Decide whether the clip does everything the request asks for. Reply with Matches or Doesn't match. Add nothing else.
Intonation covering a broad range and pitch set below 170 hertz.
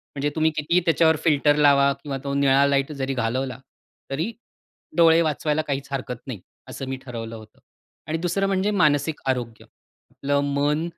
Doesn't match